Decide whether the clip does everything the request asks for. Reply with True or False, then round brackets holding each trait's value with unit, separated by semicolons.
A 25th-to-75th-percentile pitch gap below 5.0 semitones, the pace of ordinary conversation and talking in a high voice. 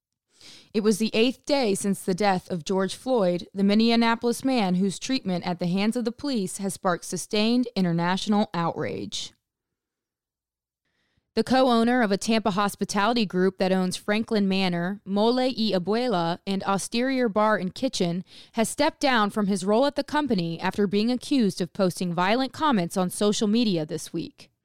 True (4.0 semitones; 165 wpm; 205 Hz)